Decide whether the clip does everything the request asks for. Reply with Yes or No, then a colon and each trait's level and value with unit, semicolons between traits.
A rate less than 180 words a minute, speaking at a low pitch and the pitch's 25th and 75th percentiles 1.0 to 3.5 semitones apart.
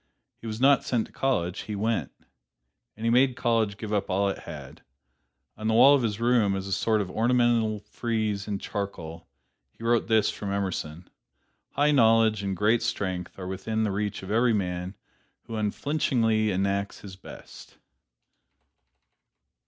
Yes: average, 160 wpm; low, 110 Hz; average, 2.7 semitones